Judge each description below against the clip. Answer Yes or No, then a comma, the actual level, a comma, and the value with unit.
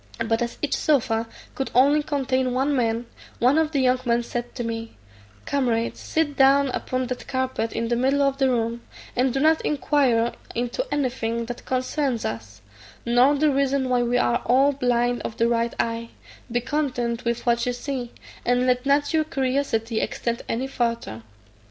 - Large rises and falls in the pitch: No, average, 2.7 semitones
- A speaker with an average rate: Yes, average, 175 wpm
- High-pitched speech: Yes, very high, 250 Hz